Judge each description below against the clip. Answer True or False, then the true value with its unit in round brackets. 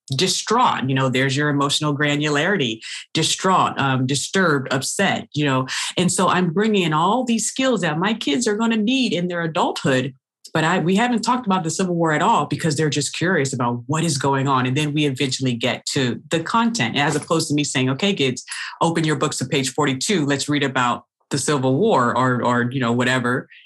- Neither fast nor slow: False (210 wpm)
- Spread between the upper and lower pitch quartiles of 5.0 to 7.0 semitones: True (5.4 semitones)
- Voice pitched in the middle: True (150 Hz)